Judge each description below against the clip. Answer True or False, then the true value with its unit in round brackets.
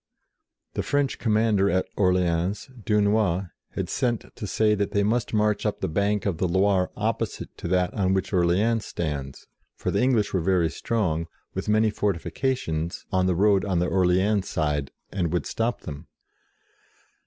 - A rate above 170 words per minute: True (185 wpm)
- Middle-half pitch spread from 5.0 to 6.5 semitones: False (3.3 semitones)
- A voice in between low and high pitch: False (95 Hz)